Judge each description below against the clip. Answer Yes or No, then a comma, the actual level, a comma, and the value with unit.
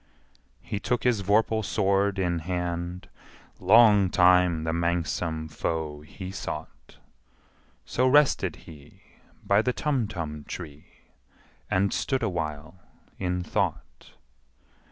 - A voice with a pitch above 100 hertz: No, very low, 90 Hz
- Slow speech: Yes, slow, 105 wpm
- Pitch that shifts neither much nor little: Yes, average, 4.0 semitones